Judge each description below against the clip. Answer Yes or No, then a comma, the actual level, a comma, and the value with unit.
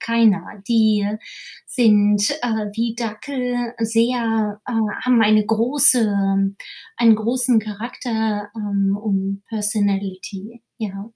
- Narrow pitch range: Yes, narrow, 2.2 semitones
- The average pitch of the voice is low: No, high, 220 Hz